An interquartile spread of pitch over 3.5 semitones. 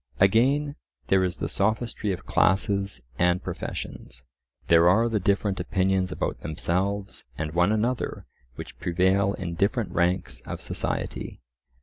No: average, 2.8 semitones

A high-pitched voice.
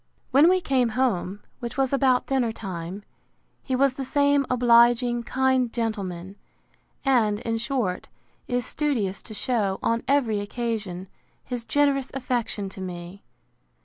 Yes: high, 240 Hz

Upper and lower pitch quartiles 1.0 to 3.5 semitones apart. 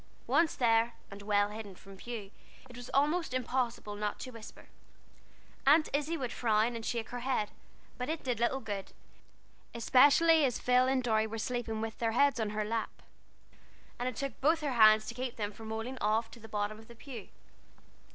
Yes: average, 3.0 semitones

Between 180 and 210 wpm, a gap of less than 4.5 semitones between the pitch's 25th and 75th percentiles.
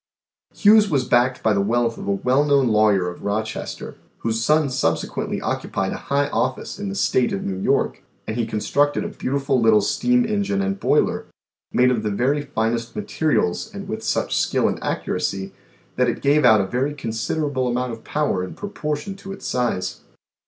No: average, 190 wpm; average, 5.2 semitones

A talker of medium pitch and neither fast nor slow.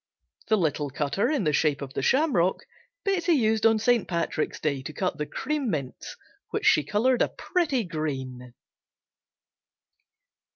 Yes: medium, 180 Hz; average, 150 wpm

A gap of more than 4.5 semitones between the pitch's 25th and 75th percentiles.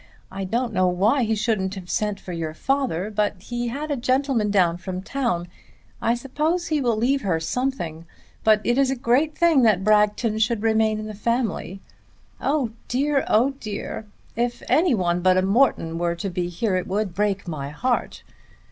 Yes: average, 5.2 semitones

